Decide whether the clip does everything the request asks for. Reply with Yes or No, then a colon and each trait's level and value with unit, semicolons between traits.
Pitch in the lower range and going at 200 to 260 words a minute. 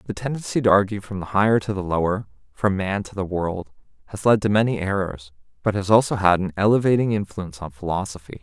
Yes: low, 100 Hz; fast, 205 wpm